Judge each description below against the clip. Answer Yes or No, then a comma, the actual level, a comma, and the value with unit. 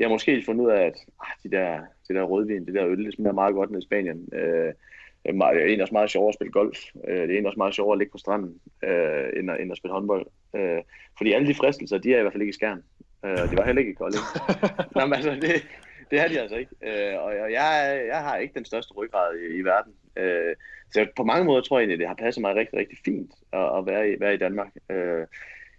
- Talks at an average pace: No, fast, 245 wpm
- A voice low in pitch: Yes, low, 115 Hz